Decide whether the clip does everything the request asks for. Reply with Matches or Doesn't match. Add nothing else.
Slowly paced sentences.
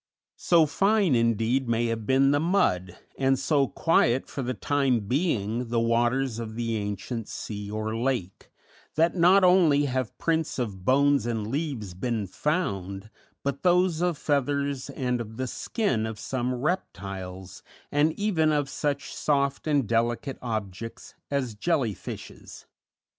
Doesn't match